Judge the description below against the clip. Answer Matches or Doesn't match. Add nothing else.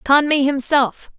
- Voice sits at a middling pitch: Doesn't match